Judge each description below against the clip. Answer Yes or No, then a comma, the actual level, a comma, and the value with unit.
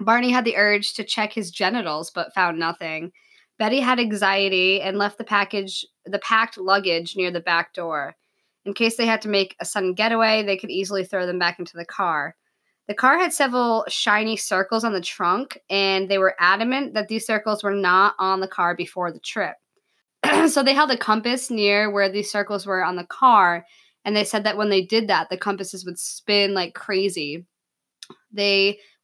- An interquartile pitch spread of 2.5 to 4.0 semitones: Yes, average, 2.9 semitones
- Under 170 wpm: No, average, 195 wpm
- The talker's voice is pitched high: Yes, high, 200 Hz